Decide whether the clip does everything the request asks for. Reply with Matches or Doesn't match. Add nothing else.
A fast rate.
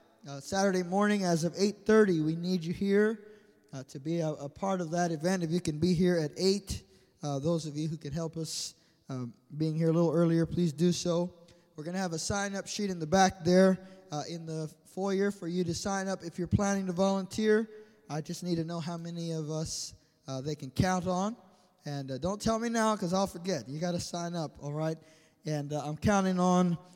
Matches